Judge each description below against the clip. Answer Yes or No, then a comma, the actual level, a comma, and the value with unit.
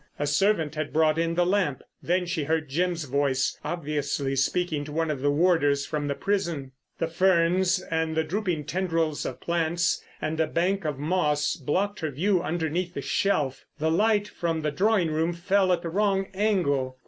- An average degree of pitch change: Yes, average, 3.6 semitones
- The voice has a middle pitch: Yes, medium, 165 Hz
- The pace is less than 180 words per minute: No, average, 185 wpm